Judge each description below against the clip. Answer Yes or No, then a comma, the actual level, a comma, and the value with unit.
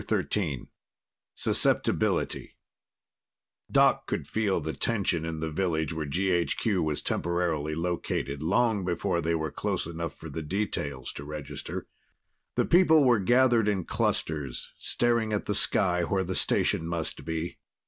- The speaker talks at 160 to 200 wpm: No, slow, 135 wpm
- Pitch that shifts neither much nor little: Yes, average, 4.4 semitones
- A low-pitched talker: Yes, very low, 85 Hz